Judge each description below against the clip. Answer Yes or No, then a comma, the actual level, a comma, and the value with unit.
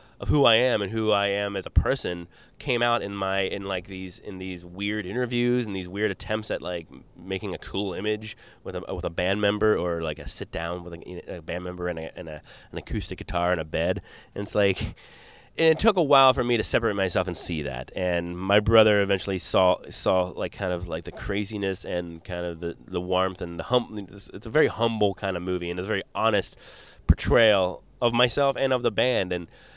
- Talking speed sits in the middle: No, fast, 230 wpm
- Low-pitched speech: Yes, very low, 95 Hz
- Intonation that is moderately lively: Yes, average, 3.5 semitones